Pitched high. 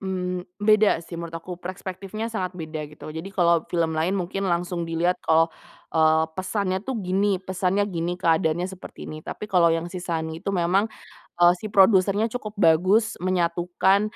No: medium, 180 Hz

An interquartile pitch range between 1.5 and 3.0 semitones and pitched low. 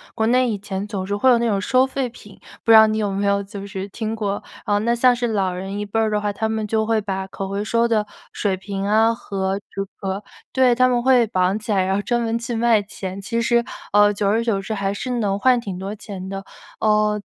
No: average, 2.7 semitones; high, 210 Hz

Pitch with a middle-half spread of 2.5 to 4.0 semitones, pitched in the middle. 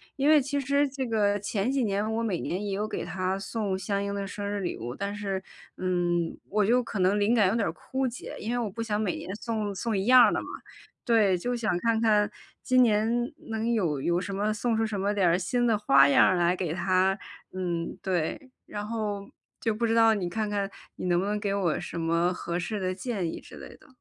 No: average, 3.5 semitones; high, 205 Hz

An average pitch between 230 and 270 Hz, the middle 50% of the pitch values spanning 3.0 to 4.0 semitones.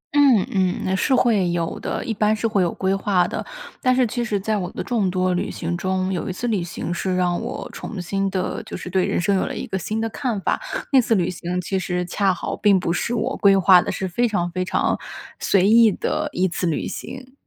No: high, 190 Hz; average, 3.5 semitones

